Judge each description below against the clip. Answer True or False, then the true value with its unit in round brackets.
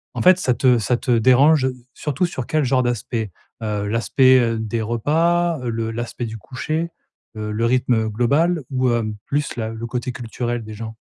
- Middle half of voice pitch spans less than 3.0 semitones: False (3.3 semitones)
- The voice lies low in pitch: True (120 Hz)